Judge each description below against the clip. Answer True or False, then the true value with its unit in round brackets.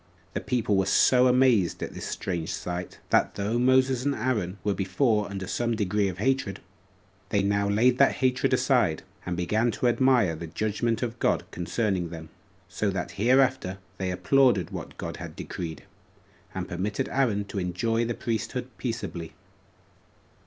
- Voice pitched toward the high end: False (105 Hz)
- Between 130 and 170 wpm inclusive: True (160 wpm)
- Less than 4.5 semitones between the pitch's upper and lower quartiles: False (5.1 semitones)